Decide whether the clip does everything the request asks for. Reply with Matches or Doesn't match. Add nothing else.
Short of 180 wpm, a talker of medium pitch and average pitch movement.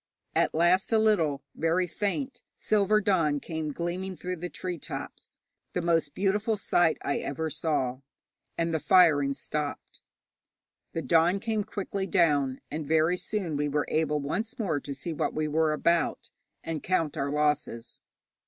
Matches